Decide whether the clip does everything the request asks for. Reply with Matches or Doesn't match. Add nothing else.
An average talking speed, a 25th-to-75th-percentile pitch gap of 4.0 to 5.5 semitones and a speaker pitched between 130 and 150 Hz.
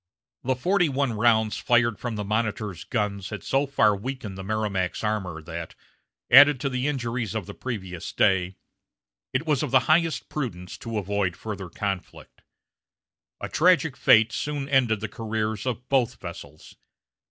Doesn't match